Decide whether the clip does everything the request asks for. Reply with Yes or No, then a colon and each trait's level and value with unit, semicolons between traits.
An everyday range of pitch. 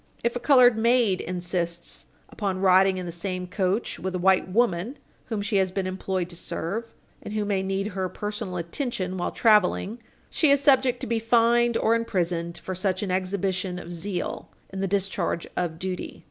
Yes: average, 3.5 semitones